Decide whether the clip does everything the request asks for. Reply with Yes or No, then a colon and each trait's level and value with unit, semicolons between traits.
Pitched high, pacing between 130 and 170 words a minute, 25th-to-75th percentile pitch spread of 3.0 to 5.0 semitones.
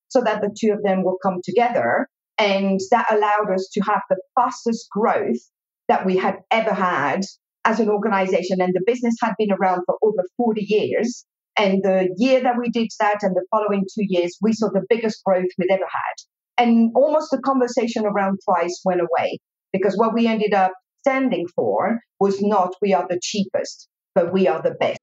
No: high, 205 Hz; average, 195 wpm; average, 3.4 semitones